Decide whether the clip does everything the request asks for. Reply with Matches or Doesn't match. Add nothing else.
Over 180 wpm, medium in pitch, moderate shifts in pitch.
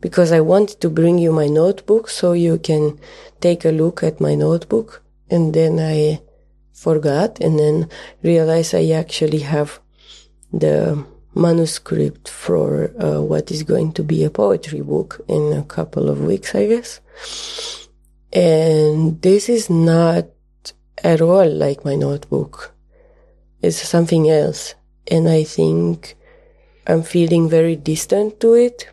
Doesn't match